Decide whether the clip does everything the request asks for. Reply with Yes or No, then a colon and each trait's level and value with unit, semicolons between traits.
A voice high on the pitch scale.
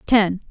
Yes: high, 200 Hz